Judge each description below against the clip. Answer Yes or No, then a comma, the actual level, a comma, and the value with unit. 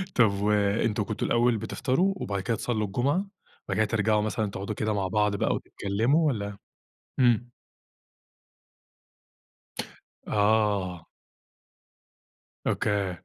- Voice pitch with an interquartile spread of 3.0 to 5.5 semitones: No, narrow, 2.4 semitones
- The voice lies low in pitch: Yes, low, 105 Hz